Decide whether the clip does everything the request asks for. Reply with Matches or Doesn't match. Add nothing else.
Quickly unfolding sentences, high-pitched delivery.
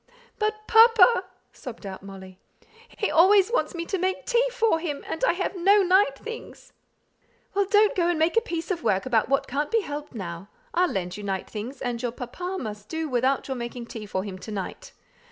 Matches